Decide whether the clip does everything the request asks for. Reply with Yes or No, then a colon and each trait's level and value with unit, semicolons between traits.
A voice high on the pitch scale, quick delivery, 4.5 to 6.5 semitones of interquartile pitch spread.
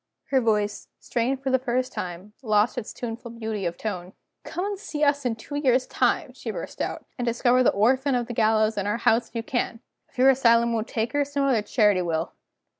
No: high, 235 Hz; fast, 220 wpm; average, 3.3 semitones